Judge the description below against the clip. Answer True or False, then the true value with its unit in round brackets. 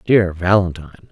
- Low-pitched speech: True (90 Hz)